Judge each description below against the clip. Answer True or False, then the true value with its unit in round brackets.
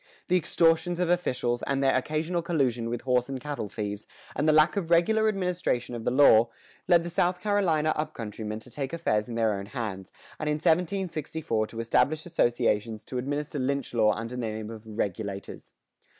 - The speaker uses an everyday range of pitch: False (6.4 semitones)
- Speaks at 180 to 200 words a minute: True (190 wpm)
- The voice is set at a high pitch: False (135 Hz)